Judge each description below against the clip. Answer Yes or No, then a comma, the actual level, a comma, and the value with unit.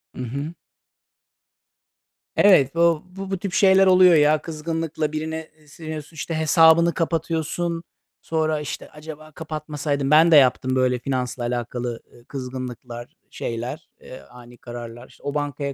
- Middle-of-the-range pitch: Yes, medium, 150 Hz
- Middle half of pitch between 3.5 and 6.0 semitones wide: Yes, average, 4.2 semitones